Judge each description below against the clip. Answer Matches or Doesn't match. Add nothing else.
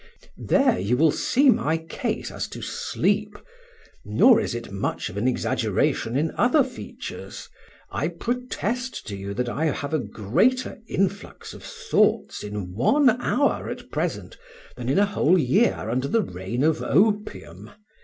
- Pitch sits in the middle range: Matches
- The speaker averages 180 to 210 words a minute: Doesn't match